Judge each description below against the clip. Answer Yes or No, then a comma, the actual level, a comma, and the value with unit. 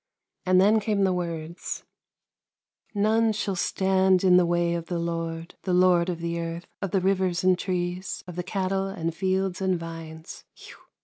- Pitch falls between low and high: Yes, medium, 180 Hz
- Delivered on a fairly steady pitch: Yes, narrow, 2.0 semitones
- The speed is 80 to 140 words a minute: No, average, 180 wpm